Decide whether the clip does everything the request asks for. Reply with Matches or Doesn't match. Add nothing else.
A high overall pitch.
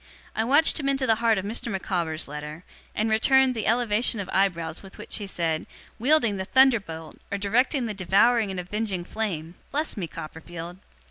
Matches